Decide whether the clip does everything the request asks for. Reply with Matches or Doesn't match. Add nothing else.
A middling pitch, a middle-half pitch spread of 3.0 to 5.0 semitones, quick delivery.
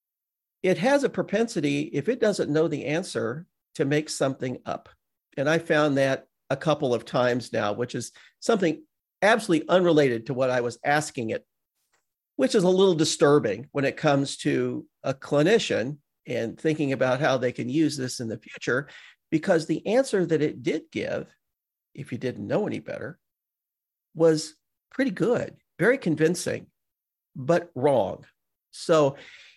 Doesn't match